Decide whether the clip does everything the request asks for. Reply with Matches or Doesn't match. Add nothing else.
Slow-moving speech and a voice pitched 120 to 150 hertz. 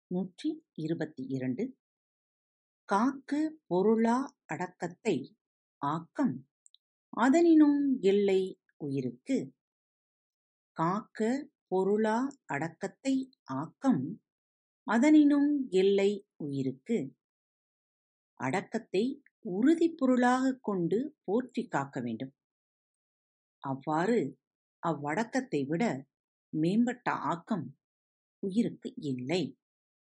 Doesn't match